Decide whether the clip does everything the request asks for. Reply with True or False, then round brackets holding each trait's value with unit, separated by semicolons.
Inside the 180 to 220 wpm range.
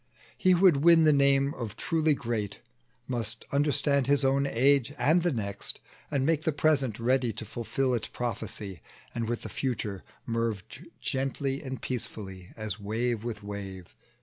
False (160 wpm)